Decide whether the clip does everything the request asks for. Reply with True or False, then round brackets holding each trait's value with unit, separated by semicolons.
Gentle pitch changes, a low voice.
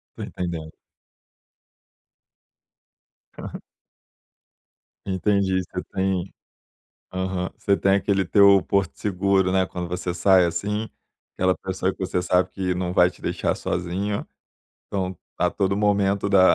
True (1.5 semitones; 95 Hz)